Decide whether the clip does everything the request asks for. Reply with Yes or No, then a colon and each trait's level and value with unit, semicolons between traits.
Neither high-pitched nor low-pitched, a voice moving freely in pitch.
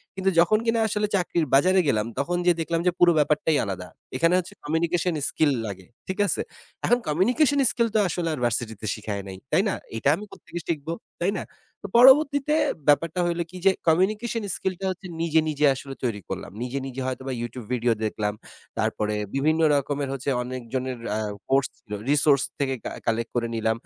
Yes: medium, 150 Hz; wide, 6.5 semitones